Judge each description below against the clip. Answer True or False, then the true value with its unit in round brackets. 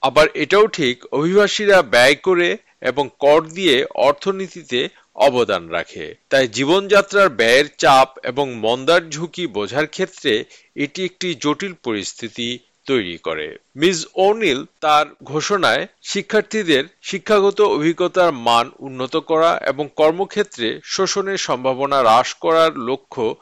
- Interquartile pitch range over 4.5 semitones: True (5.6 semitones)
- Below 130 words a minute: True (115 wpm)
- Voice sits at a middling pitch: True (170 Hz)